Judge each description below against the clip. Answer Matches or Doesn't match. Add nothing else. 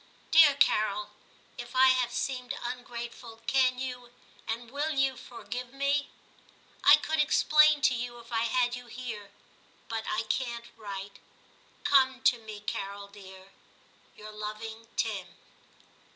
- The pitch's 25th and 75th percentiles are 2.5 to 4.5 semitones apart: Matches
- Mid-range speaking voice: Doesn't match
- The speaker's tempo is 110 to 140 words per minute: Matches